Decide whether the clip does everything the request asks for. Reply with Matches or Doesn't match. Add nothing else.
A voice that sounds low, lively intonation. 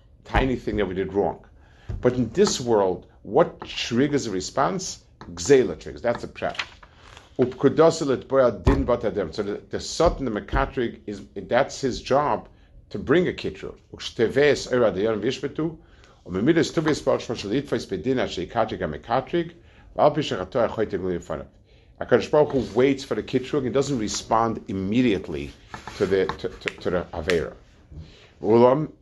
Matches